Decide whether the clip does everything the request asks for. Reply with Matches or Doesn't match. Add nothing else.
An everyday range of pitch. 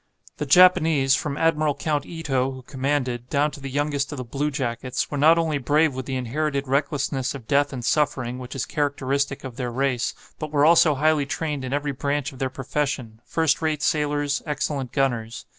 Doesn't match